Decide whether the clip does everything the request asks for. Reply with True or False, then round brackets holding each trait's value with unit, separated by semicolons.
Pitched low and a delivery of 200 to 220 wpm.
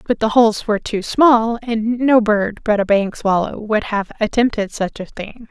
False (220 Hz; 205 wpm)